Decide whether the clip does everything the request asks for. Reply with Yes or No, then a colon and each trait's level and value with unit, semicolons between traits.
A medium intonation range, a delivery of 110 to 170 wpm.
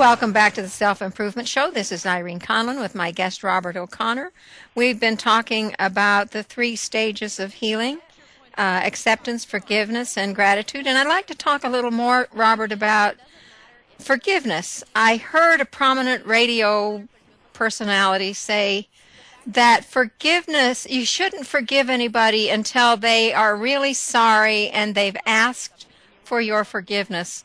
Yes: average, 3.3 semitones; average, 140 wpm